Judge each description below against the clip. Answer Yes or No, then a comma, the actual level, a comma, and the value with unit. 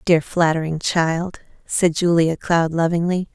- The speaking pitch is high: No, medium, 165 Hz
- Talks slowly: Yes, slow, 125 wpm